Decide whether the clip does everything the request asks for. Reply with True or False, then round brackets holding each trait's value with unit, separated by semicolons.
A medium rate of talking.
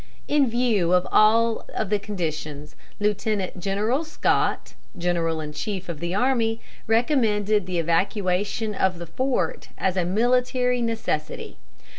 False (125 wpm)